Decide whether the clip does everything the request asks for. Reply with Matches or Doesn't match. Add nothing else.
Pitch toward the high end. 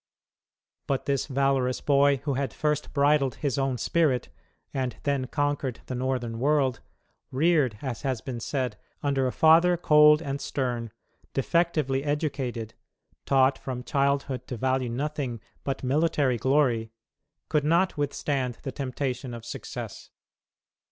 Doesn't match